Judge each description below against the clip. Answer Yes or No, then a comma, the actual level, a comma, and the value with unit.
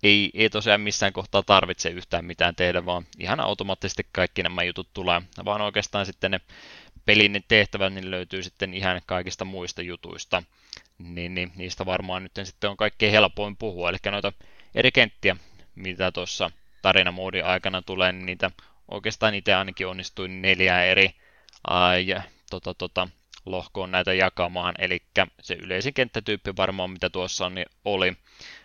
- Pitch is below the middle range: Yes, very low, 95 Hz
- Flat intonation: Yes, narrow, 1.6 semitones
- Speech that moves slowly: No, average, 150 wpm